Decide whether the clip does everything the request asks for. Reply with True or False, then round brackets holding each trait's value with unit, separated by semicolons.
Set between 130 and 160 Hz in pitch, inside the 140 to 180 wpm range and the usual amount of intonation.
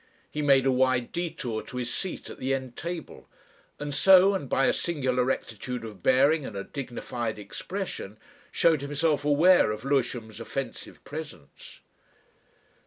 True (135 Hz; 150 wpm; 4.0 semitones)